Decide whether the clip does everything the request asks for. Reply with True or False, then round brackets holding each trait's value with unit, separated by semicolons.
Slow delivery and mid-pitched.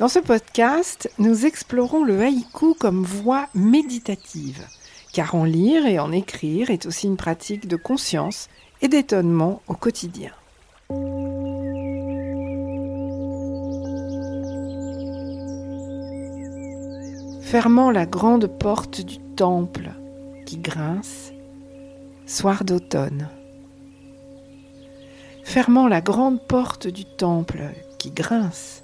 True (90 wpm; 155 Hz)